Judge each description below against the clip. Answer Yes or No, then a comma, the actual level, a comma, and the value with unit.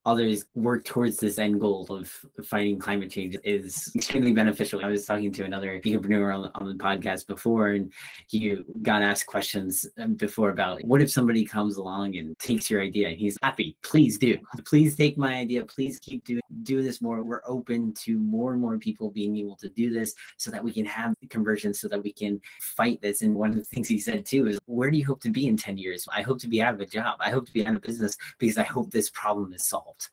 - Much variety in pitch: No, average, 3.4 semitones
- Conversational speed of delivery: No, fast, 240 wpm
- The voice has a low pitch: Yes, low, 110 Hz